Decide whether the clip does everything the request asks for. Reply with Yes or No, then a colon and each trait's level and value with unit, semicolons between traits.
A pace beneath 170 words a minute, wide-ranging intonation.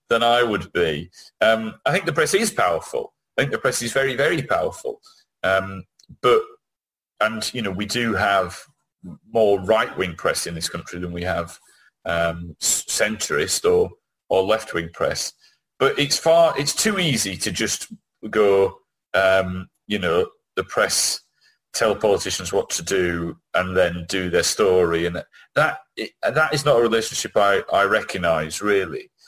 Yes: average, 160 wpm; wide, 8.3 semitones